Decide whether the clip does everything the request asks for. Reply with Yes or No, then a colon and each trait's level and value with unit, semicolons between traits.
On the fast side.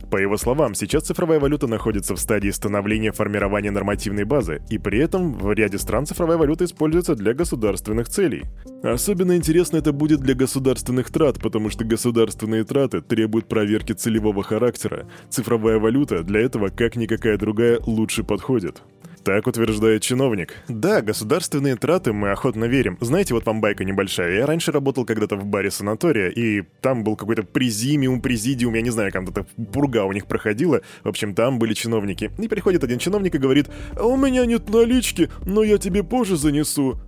Yes: fast, 170 wpm